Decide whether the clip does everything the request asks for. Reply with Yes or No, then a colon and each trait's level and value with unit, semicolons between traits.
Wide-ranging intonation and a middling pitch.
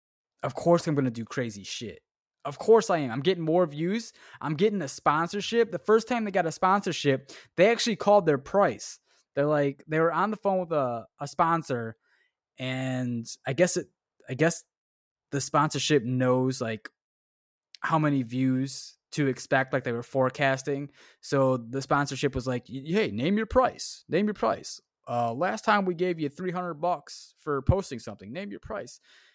Yes: wide, 5.8 semitones; medium, 145 Hz